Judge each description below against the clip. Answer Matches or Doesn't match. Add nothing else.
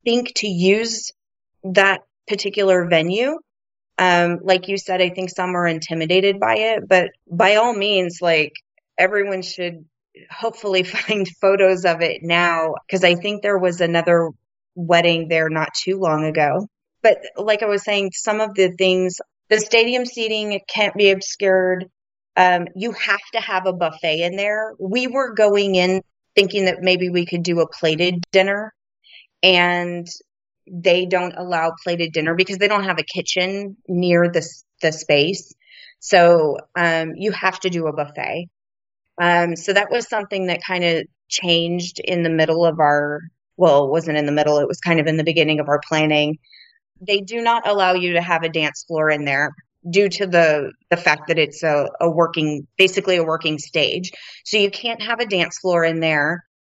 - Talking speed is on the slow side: Doesn't match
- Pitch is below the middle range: Doesn't match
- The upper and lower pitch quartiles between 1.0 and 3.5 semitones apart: Matches